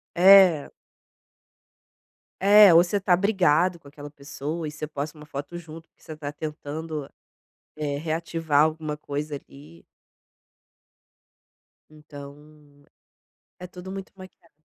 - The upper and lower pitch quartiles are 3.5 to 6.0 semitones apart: No, average, 3.0 semitones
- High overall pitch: No, medium, 155 Hz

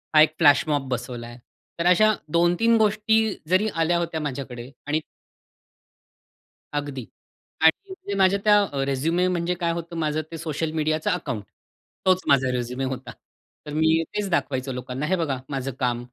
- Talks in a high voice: No, medium, 155 Hz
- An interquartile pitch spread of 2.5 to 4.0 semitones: No, average, 4.8 semitones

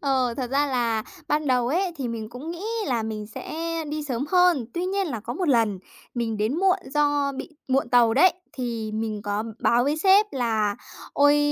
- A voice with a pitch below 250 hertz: No, very high, 255 Hz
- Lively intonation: No, average, 4.7 semitones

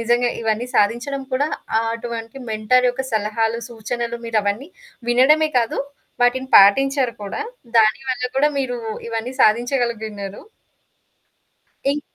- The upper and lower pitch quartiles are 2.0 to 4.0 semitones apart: Yes, narrow, 2.6 semitones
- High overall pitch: Yes, high, 235 Hz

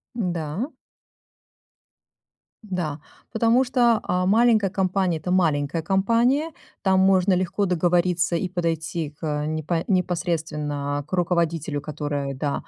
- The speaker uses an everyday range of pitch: Yes, average, 3.7 semitones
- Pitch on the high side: No, medium, 175 Hz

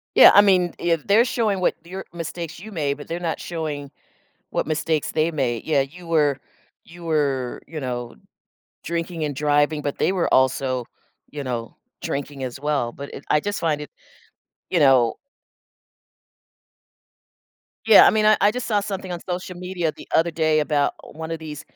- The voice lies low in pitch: No, medium, 155 Hz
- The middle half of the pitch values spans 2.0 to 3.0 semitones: No, average, 3.7 semitones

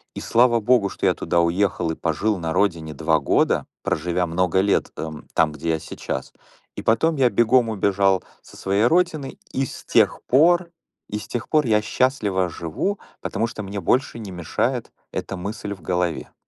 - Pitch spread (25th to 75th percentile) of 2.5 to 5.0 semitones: No, wide, 5.4 semitones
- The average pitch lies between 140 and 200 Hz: No, low, 100 Hz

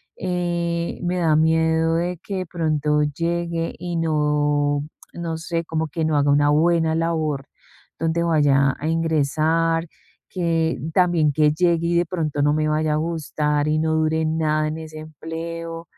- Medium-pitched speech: Yes, medium, 160 Hz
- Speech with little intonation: Yes, narrow, 1.7 semitones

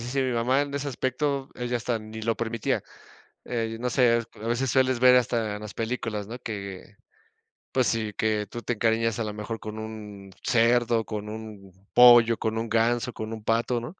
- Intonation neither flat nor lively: No, narrow, 2.0 semitones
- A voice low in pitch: Yes, low, 115 Hz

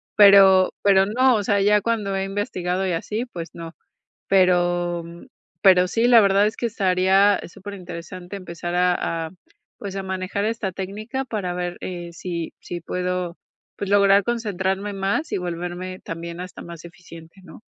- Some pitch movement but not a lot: No, narrow, 2.3 semitones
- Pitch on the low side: No, high, 190 Hz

